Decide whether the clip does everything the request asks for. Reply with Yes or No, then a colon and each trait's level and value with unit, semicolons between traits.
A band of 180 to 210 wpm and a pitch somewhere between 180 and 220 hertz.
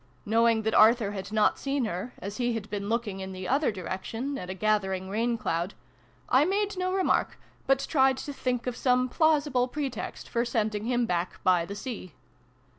No: average, 190 wpm; high, 230 Hz